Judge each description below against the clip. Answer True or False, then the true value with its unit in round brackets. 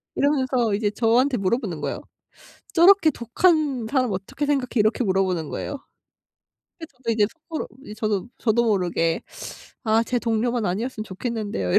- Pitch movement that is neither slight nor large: True (4.2 semitones)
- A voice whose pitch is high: True (230 Hz)